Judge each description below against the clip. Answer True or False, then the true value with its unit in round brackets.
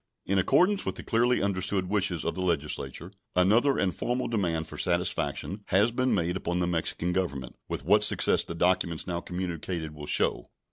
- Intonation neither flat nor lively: True (3.1 semitones)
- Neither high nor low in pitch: False (90 Hz)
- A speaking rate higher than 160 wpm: True (180 wpm)